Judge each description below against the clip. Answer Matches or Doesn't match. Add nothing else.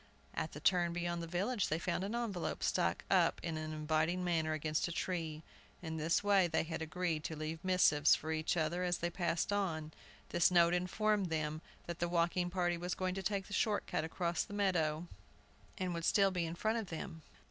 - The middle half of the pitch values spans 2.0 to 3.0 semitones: Matches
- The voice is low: Doesn't match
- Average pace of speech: Doesn't match